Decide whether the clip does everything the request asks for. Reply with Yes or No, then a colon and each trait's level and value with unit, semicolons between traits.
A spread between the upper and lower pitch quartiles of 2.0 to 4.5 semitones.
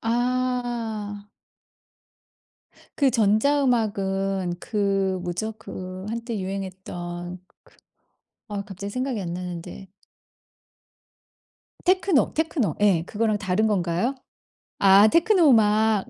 Yes: average, 3.9 semitones